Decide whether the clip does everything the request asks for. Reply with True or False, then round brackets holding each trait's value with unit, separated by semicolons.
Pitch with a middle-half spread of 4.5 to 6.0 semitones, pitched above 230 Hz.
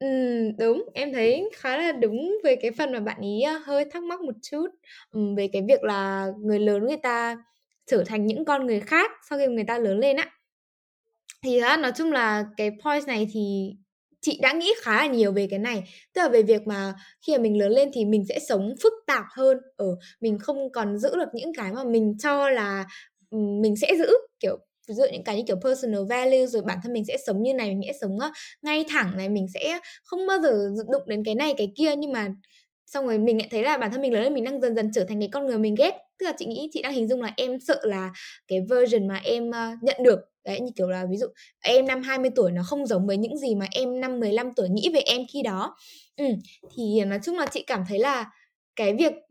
True (5.2 semitones; 240 Hz)